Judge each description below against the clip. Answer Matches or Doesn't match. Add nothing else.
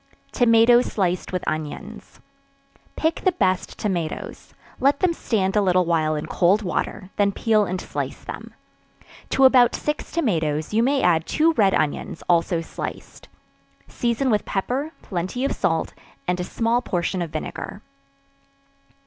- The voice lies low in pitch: Doesn't match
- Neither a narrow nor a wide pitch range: Doesn't match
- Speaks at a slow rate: Doesn't match